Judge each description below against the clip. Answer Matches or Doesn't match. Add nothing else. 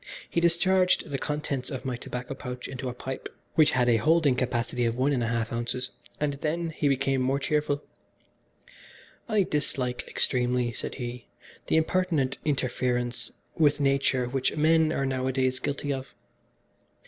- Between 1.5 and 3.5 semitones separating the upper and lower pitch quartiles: Matches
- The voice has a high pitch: Doesn't match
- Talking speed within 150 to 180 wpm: Matches